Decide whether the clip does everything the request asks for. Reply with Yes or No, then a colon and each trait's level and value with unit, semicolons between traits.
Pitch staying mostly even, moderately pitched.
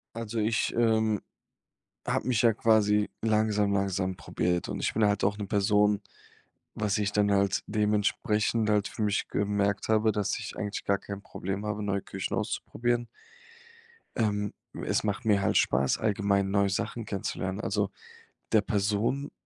No: narrow, 1.5 semitones; low, 105 Hz